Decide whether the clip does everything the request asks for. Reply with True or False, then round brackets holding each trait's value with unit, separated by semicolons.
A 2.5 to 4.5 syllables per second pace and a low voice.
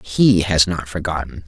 True (4.2 syllables/s; 85 Hz)